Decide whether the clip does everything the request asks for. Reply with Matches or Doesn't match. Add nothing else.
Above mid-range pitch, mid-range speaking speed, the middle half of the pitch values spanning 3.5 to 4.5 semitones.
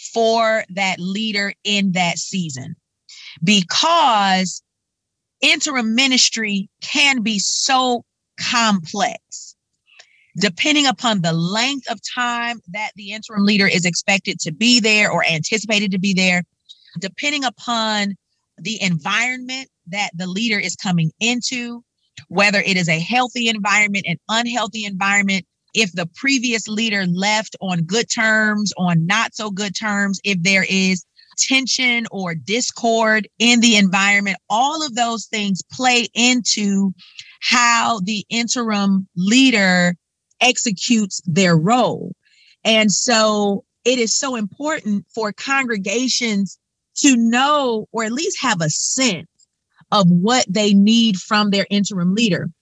Doesn't match